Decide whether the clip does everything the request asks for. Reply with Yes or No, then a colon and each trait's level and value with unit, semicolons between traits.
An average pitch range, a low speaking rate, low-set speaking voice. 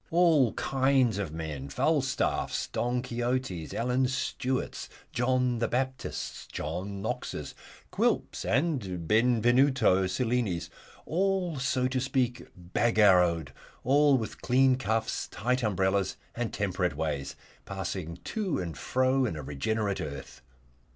No: wide, 5.9 semitones; slow, 115 wpm; low, 120 Hz